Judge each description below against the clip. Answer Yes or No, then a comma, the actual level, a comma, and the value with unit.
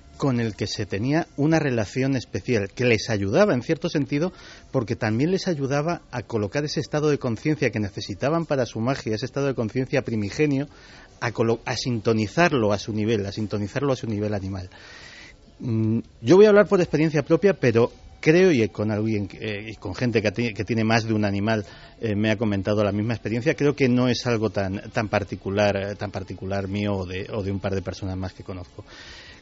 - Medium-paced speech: No, fast, 195 wpm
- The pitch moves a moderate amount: Yes, average, 4.6 semitones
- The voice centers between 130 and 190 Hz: No, low, 115 Hz